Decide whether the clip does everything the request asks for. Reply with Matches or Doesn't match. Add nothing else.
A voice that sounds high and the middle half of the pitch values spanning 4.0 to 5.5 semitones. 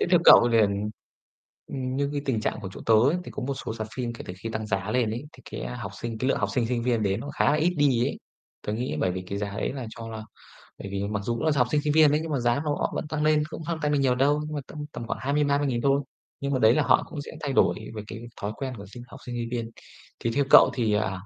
Doesn't match